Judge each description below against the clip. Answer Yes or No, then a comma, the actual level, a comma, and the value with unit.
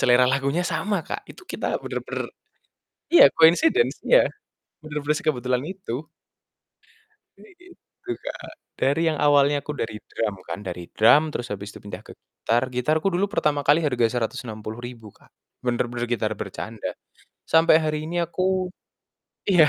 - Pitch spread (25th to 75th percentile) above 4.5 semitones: Yes, average, 5.3 semitones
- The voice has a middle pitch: Yes, medium, 145 Hz